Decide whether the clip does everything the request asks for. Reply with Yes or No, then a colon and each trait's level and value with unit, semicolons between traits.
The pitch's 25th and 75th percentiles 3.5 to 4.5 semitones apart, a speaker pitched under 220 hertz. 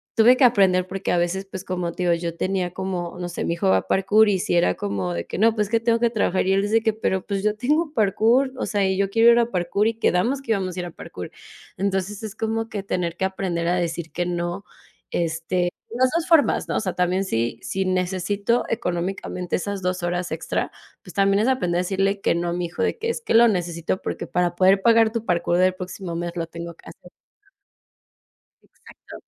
Yes: average, 3.8 semitones; high, 190 Hz